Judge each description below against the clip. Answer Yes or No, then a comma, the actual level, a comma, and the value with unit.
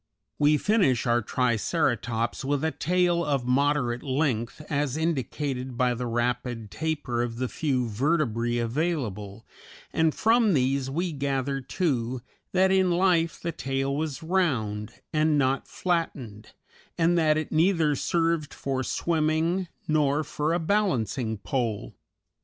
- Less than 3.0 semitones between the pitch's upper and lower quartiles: No, average, 5.0 semitones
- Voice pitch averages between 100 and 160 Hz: Yes, medium, 140 Hz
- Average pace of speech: No, slow, 130 wpm